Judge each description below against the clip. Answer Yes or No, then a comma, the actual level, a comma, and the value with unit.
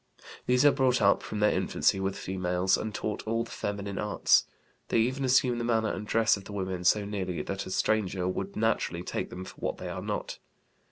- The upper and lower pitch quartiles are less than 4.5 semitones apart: Yes, average, 3.2 semitones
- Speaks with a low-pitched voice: Yes, low, 105 Hz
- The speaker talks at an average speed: No, fast, 215 wpm